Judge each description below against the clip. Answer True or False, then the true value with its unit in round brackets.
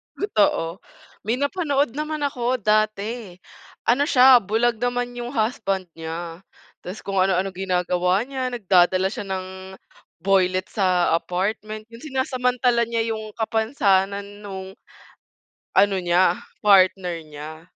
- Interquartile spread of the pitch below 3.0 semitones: False (4.7 semitones)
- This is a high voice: True (205 Hz)